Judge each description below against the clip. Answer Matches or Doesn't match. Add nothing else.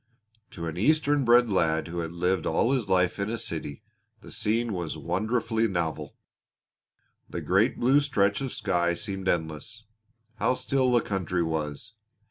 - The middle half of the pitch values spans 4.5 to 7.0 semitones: Matches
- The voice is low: Matches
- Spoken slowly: Doesn't match